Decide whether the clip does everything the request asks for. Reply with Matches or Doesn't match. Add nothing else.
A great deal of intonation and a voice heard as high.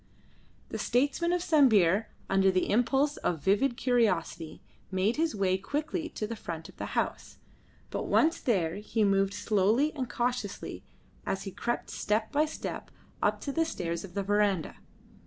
Matches